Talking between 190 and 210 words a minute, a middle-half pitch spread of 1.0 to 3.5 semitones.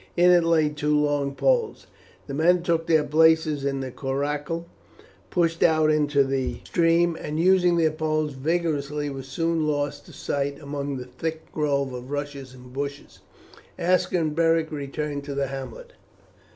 No: average, 160 wpm; average, 2.8 semitones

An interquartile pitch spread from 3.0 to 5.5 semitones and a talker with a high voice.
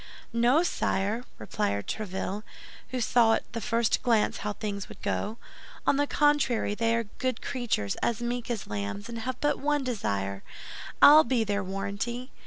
Yes: average, 3.8 semitones; high, 230 Hz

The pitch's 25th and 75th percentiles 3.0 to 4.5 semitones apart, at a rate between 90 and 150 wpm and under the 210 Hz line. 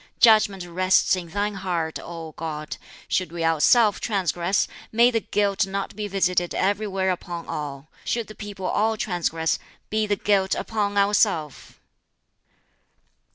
Yes: average, 3.4 semitones; slow, 135 wpm; high, 190 Hz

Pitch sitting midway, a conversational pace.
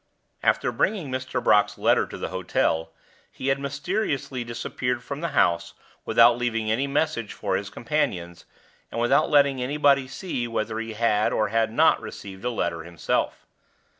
No: low, 120 Hz; average, 160 wpm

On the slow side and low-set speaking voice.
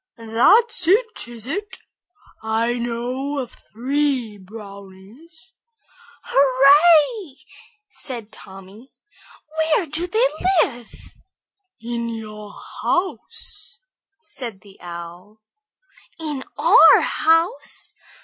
No: slow, 80 wpm; very high, 250 Hz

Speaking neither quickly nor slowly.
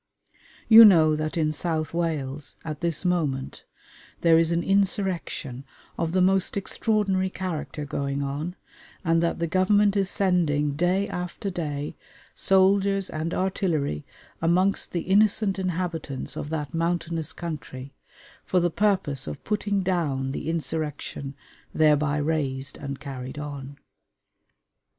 No: slow, 125 wpm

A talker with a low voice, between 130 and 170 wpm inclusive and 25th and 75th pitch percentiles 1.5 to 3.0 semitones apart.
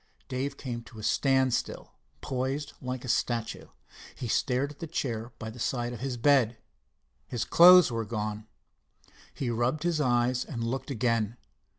Yes: low, 125 Hz; average, 160 wpm; average, 2.7 semitones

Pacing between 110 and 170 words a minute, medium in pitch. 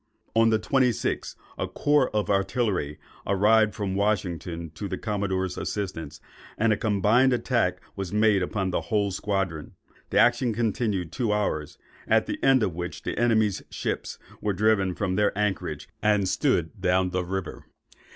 No: average, 155 wpm; low, 100 Hz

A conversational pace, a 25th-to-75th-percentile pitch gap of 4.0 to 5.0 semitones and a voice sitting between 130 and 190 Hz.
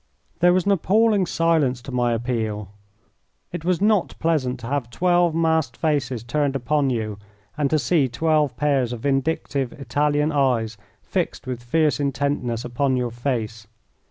Yes: average, 155 wpm; average, 4.7 semitones; medium, 140 Hz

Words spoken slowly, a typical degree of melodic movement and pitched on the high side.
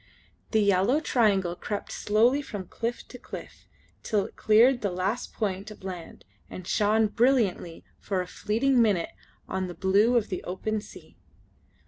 No: average, 155 wpm; average, 3.6 semitones; high, 210 Hz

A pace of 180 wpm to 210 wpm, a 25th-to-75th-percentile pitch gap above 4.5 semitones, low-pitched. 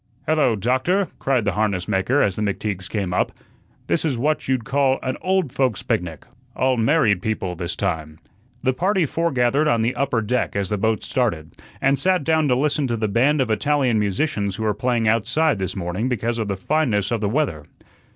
Yes: average, 200 wpm; wide, 5.4 semitones; low, 120 Hz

